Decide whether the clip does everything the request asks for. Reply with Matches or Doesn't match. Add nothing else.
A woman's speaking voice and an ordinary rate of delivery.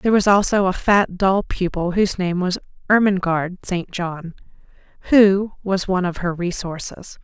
Matches